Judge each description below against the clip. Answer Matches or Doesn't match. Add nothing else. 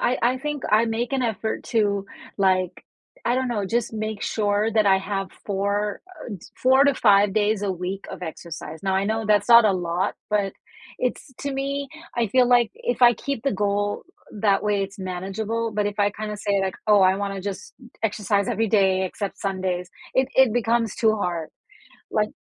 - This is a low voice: Doesn't match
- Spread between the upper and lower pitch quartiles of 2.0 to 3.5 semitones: Matches